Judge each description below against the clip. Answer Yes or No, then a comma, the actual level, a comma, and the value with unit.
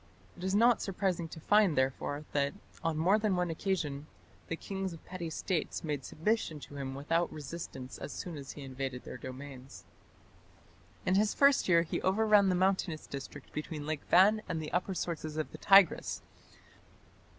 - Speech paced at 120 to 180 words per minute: Yes, average, 175 wpm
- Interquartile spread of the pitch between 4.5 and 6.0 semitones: Yes, average, 4.8 semitones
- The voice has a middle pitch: Yes, medium, 165 Hz